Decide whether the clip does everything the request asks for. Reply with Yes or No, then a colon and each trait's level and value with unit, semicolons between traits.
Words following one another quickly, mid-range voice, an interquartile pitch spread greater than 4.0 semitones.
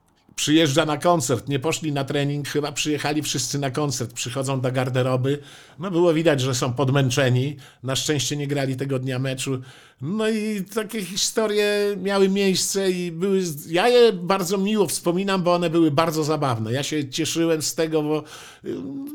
Yes: fast, 165 wpm; medium, 155 Hz; average, 5.1 semitones